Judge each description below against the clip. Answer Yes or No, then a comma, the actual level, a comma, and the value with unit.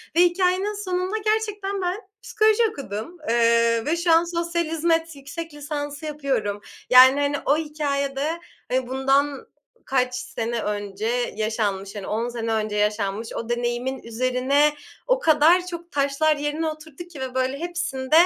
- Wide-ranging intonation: Yes, wide, 5.9 semitones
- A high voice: Yes, very high, 285 Hz